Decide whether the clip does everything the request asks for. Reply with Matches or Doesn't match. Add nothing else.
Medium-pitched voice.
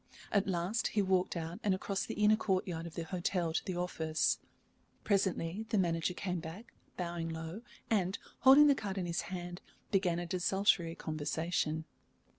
Matches